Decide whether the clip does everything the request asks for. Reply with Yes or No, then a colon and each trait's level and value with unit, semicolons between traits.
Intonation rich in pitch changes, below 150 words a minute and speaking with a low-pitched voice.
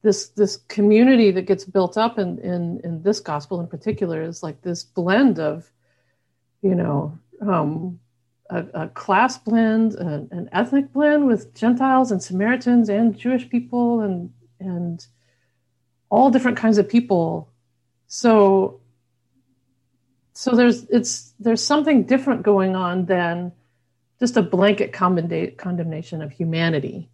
No: wide, 6.7 semitones; slow, 135 wpm; medium, 185 Hz